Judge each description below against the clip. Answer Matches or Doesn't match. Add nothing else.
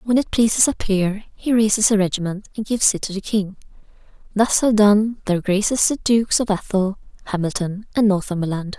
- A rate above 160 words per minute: Matches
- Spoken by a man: Doesn't match